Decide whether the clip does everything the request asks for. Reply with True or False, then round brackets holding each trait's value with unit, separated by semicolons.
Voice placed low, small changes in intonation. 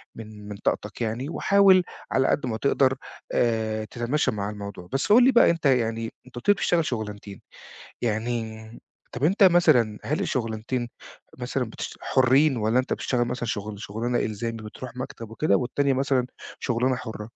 False (120 Hz; 3.5 semitones)